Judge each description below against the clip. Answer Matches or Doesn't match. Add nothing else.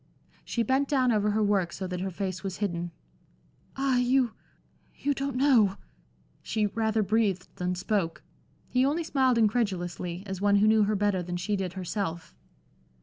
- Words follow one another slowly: Doesn't match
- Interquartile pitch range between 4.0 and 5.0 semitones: Matches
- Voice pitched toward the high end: Matches